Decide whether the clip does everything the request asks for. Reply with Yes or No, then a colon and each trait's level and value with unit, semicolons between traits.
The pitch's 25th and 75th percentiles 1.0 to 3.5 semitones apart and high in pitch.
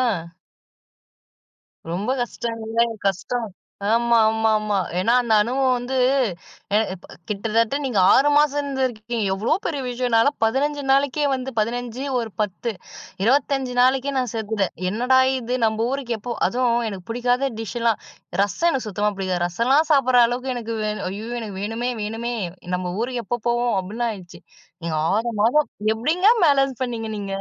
Yes: average, 3.0 semitones; high, 235 Hz